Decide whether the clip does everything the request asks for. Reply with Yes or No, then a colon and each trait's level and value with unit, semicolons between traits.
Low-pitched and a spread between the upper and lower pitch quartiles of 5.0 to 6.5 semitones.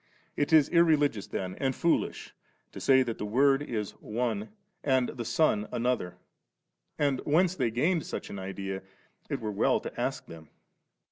Yes: low, 125 Hz; wide, 5.6 semitones